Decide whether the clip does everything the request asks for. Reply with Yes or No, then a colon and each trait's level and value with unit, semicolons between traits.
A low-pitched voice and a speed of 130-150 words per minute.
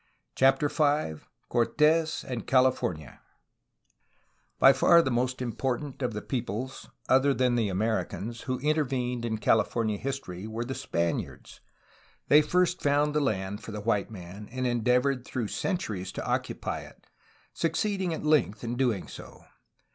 Yes: low, 125 Hz; average, 140 wpm